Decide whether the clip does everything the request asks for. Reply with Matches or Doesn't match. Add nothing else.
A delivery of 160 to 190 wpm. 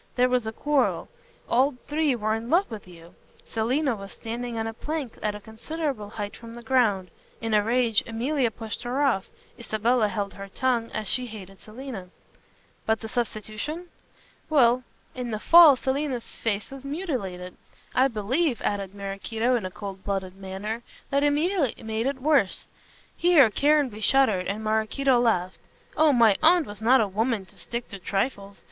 Matches